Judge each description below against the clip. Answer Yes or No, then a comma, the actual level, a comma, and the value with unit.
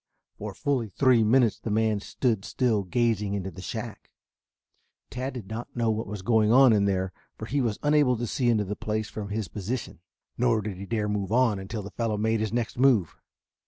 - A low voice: Yes, low, 110 Hz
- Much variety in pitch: No, average, 2.9 semitones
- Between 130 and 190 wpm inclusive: No, fast, 205 wpm